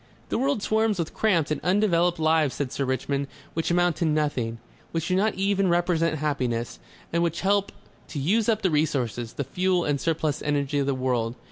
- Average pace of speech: Yes, average, 195 wpm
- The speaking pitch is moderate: Yes, medium, 160 Hz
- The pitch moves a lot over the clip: No, average, 4.6 semitones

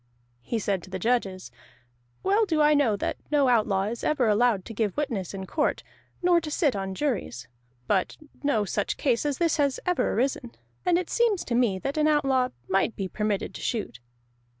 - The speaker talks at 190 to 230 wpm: Yes, average, 195 wpm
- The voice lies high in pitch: Yes, high, 240 Hz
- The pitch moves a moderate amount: No, wide, 6.8 semitones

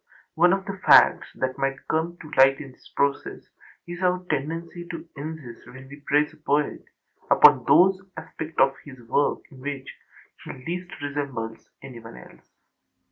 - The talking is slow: No, average, 160 wpm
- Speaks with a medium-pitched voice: Yes, medium, 145 Hz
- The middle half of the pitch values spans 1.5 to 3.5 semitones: No, average, 3.9 semitones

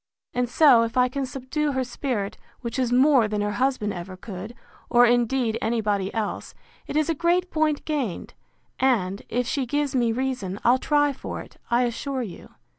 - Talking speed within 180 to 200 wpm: Yes, average, 190 wpm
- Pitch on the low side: No, high, 245 Hz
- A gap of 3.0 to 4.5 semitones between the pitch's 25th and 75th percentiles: Yes, average, 3.7 semitones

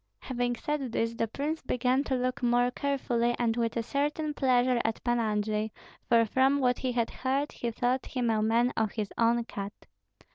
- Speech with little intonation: Yes, narrow, 2.2 semitones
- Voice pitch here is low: No, high, 245 Hz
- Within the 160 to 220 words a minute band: Yes, average, 190 wpm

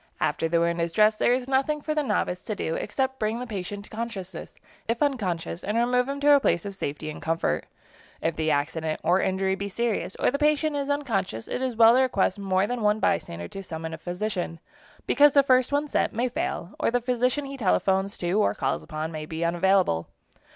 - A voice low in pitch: No, high, 205 Hz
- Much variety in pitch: Yes, wide, 6.8 semitones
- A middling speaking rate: No, fast, 220 wpm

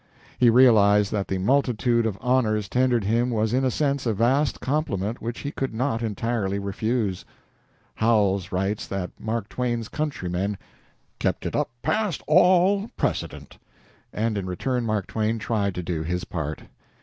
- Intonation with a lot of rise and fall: No, average, 4.2 semitones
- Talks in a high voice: No, low, 115 Hz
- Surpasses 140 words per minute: Yes, average, 155 wpm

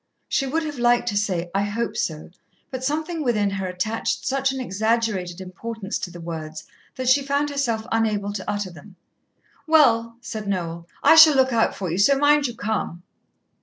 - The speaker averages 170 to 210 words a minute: Yes, average, 185 wpm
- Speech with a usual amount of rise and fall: No, wide, 5.7 semitones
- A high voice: Yes, high, 225 Hz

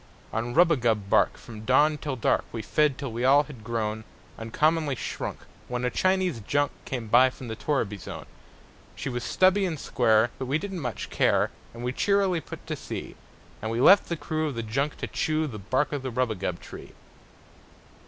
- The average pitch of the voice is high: No, low, 130 Hz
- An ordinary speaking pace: Yes, average, 190 wpm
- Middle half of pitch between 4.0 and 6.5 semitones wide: Yes, average, 5.2 semitones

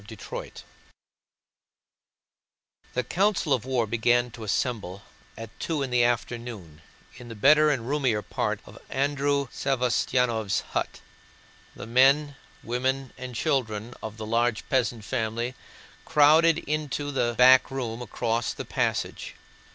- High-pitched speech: No, low, 125 Hz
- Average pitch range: Yes, average, 3.3 semitones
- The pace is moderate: No, slow, 130 wpm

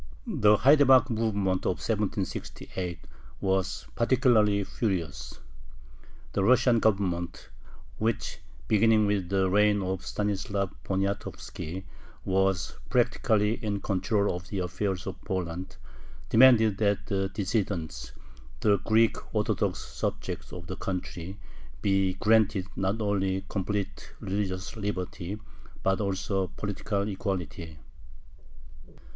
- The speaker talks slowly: Yes, slow, 105 wpm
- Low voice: Yes, low, 100 Hz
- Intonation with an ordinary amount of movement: No, narrow, 2.2 semitones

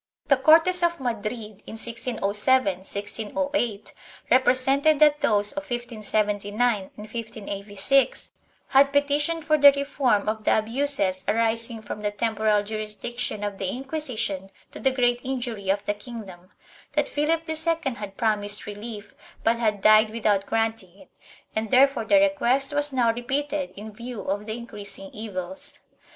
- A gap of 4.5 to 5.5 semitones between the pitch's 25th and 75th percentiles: Yes, average, 4.9 semitones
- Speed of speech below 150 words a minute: Yes, average, 140 wpm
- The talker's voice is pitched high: Yes, high, 230 Hz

